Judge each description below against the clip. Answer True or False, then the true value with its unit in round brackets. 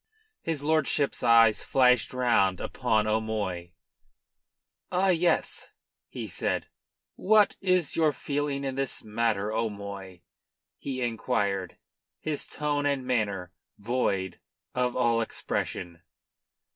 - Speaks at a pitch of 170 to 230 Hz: False (120 Hz)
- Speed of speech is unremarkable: False (105 wpm)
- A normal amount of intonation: False (5.7 semitones)